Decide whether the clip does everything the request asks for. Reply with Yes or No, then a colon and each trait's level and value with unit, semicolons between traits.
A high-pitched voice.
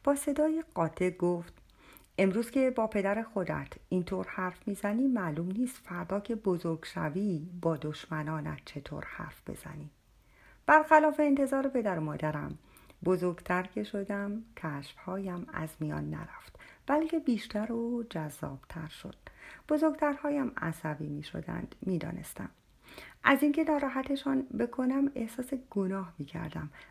Yes: high, 195 Hz